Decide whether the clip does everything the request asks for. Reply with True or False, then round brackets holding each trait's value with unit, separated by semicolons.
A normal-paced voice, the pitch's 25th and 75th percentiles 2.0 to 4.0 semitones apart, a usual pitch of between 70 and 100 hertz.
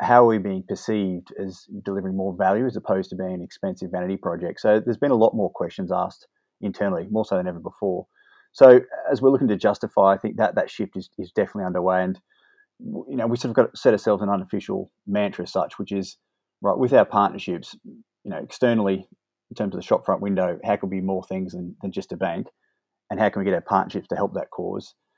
False (235 wpm; 2.9 semitones; 95 Hz)